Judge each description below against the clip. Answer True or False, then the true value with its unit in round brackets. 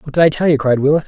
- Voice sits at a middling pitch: True (145 Hz)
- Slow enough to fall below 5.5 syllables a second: False (7.8 syllables/s)